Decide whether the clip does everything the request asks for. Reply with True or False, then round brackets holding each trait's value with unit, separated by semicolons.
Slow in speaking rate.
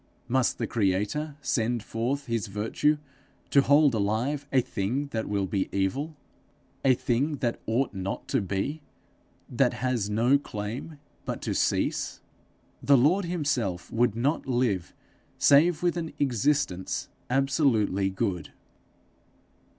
True (125 wpm)